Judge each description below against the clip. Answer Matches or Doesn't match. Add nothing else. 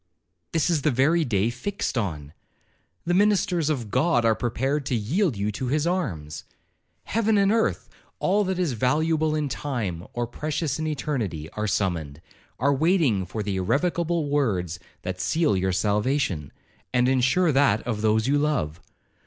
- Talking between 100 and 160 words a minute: Matches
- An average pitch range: Doesn't match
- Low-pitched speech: Matches